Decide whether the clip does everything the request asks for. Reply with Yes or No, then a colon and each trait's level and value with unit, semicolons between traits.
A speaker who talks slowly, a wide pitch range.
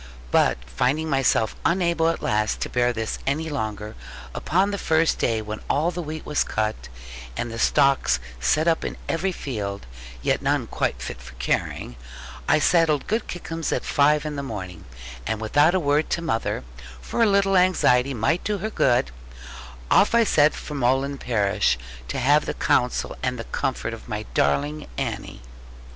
No: average, 175 wpm; wide, 6.8 semitones